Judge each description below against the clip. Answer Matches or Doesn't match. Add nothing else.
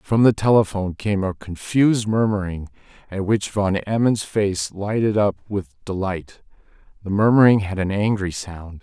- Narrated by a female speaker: Doesn't match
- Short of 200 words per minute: Matches